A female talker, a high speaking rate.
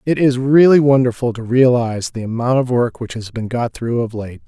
No: male; fast, 230 wpm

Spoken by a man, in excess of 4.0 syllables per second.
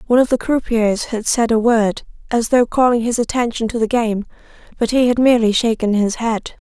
No: female; 5.5 syllables/s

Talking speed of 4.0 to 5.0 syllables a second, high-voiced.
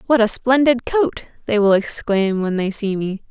Yes: 4.5 syllables/s; high, 225 Hz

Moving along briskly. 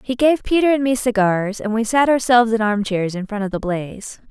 Yes: fast, 235 wpm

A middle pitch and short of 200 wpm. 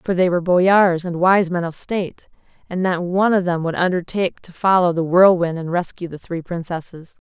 No: medium, 175 Hz; fast, 205 wpm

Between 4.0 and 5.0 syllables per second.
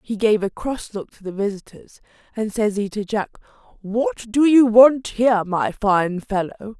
Yes: 4.5 syllables/s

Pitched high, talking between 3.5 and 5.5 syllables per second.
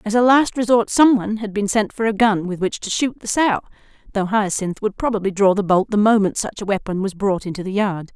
No: high, 210 Hz; 5.7 syllables/s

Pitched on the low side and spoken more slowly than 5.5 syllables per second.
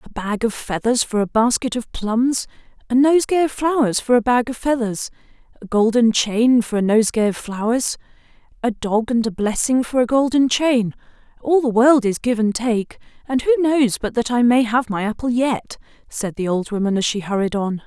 No: high, 235 Hz; 5.0 syllables/s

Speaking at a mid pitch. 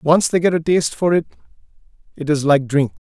Yes: medium, 155 Hz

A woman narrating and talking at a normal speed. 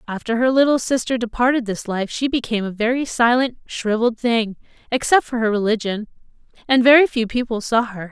Yes: female; average, 165 wpm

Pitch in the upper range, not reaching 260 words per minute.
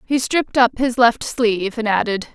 Yes: high, 235 Hz; fast, 205 wpm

